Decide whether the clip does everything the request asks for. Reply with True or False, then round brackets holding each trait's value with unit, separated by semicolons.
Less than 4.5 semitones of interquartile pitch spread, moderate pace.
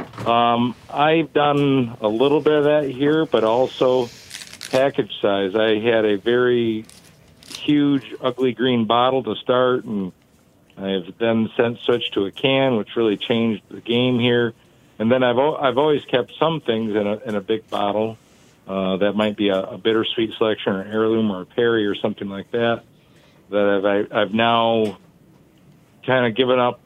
True (3.7 semitones; 170 wpm)